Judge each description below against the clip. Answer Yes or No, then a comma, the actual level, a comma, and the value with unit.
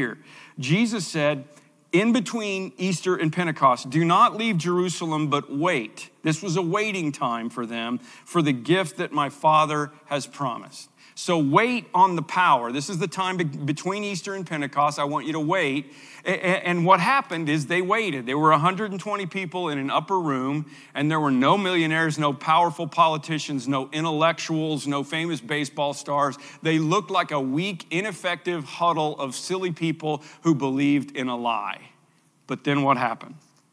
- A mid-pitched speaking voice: Yes, medium, 160 Hz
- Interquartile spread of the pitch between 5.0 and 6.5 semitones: No, average, 3.9 semitones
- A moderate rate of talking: Yes, average, 165 wpm